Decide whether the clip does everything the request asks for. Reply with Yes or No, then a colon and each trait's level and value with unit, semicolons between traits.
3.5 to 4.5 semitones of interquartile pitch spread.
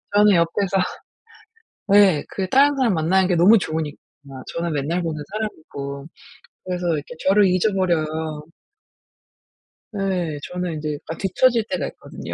Yes: average, 4.0 semitones